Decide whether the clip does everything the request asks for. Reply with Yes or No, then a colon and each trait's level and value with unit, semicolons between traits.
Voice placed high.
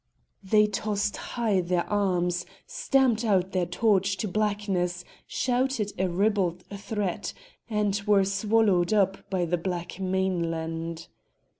Yes: high, 195 Hz